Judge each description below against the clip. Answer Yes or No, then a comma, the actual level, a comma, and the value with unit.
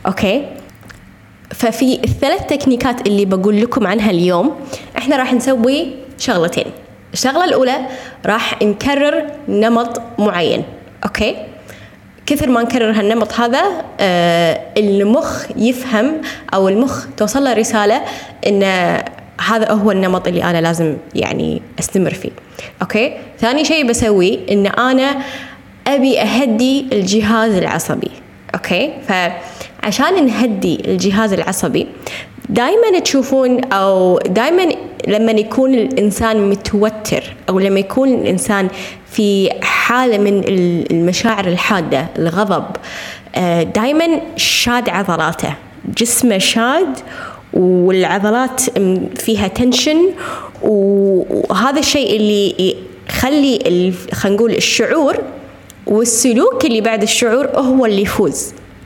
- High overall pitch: Yes, high, 225 Hz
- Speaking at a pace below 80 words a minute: No, average, 100 wpm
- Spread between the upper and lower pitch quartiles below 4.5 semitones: No, average, 4.8 semitones